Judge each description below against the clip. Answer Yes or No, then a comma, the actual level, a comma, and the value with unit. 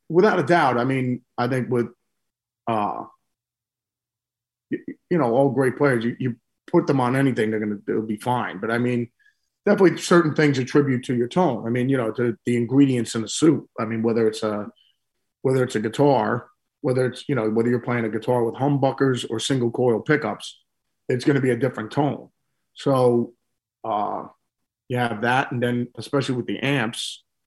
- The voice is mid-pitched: No, low, 125 Hz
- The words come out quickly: No, average, 190 wpm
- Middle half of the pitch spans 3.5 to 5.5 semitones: No, average, 2.7 semitones